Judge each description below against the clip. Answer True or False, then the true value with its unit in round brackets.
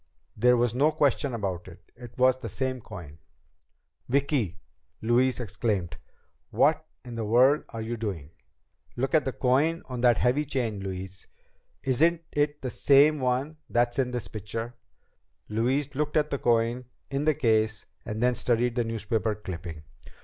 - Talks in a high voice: False (120 Hz)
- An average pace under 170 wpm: True (155 wpm)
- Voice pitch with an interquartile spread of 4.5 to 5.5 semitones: False (3.6 semitones)